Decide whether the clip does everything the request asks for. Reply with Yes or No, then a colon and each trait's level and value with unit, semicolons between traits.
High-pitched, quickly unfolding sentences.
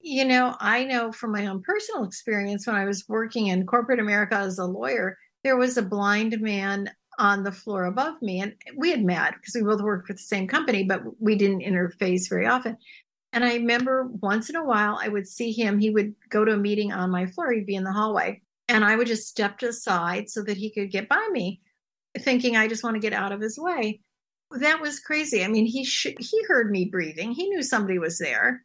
Yes: high, 215 Hz; fast, 235 wpm